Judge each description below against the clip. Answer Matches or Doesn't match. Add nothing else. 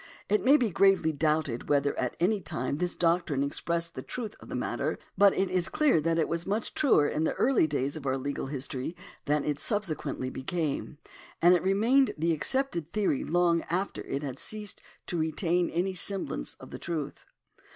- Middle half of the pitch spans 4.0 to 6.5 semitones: Matches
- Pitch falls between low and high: Matches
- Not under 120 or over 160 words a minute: Doesn't match